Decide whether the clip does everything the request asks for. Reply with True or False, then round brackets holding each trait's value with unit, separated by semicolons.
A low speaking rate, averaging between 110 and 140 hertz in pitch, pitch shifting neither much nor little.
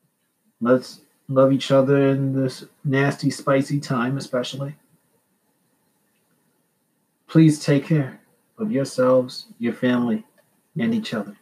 True (105 wpm; 135 Hz; 3.3 semitones)